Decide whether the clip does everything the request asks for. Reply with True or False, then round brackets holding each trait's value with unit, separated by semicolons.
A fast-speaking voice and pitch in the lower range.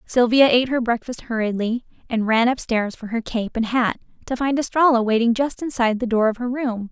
False (210 wpm; 240 Hz)